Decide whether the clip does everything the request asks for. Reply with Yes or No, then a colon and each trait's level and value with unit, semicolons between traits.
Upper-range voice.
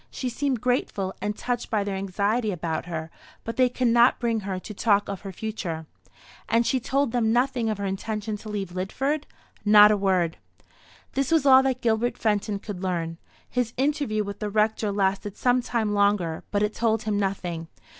Yes: high, 210 Hz